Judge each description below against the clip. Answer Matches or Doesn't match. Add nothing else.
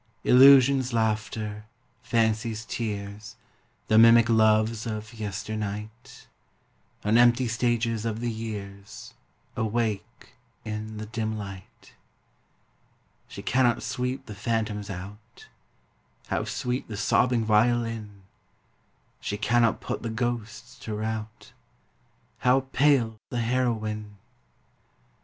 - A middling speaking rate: Doesn't match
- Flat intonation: Matches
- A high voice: Doesn't match